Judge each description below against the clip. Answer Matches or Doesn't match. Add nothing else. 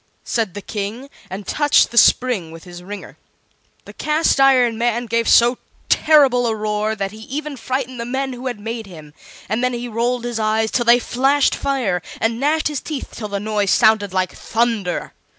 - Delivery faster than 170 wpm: Matches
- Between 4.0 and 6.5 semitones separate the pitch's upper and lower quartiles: Doesn't match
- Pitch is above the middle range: Matches